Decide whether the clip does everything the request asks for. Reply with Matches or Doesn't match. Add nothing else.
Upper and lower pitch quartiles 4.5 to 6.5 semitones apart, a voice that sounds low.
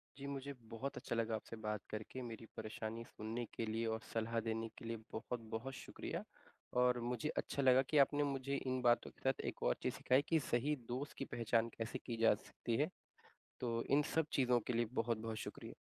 Doesn't match